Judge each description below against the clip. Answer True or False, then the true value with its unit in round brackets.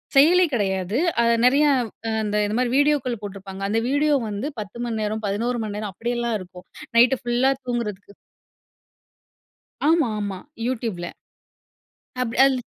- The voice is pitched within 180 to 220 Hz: False (230 Hz)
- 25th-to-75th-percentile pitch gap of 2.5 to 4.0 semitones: True (3.7 semitones)